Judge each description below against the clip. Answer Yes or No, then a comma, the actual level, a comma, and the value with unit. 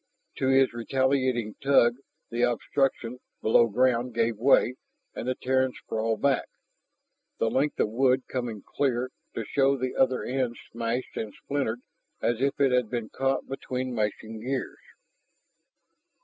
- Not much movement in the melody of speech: Yes, narrow, 2.2 semitones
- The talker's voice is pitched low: Yes, low, 125 Hz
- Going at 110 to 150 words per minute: Yes, average, 140 wpm